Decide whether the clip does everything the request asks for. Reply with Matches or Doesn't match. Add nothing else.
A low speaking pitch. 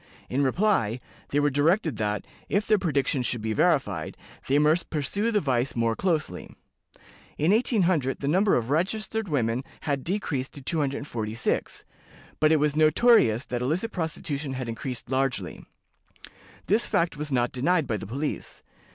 Doesn't match